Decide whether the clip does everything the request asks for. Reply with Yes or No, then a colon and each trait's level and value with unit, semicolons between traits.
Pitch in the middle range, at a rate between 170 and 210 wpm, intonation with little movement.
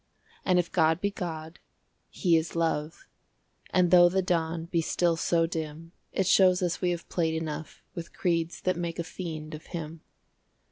Yes: medium, 165 Hz; average, 175 wpm; narrow, 1.7 semitones